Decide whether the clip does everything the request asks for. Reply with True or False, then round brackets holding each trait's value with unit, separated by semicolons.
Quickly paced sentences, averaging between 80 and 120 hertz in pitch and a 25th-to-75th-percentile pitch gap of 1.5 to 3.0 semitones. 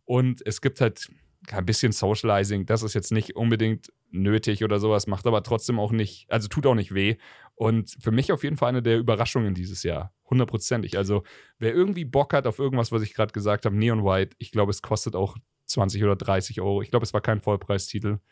True (215 wpm; 110 Hz; 2.5 semitones)